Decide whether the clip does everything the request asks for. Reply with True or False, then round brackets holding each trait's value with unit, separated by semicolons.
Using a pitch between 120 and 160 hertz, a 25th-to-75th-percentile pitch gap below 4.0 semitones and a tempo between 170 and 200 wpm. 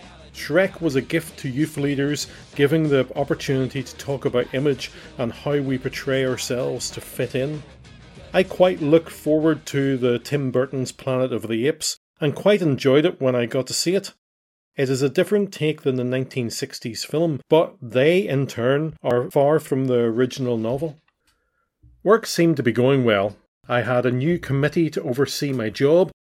True (135 Hz; 3.4 semitones; 180 wpm)